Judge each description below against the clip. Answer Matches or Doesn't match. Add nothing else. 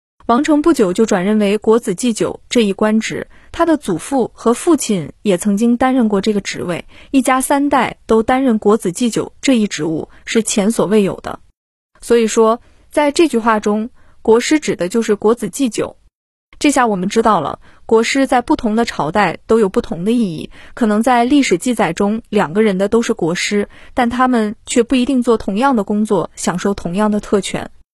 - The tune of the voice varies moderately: Matches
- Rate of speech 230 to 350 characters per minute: Matches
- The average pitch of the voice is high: Matches